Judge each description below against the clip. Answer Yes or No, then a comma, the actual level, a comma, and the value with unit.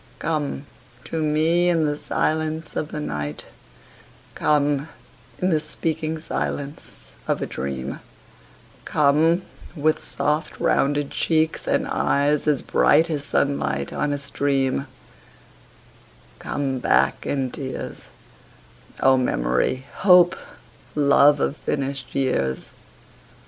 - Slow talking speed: Yes, slow, 105 wpm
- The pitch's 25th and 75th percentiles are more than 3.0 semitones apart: No, narrow, 2.5 semitones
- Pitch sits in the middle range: Yes, medium, 145 Hz